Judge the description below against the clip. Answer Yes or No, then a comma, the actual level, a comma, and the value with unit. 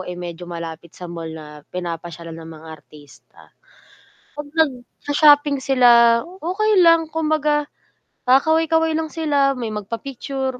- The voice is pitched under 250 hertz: No, very high, 265 Hz